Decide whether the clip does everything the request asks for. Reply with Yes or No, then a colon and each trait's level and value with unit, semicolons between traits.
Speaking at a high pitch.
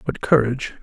No: low, 130 Hz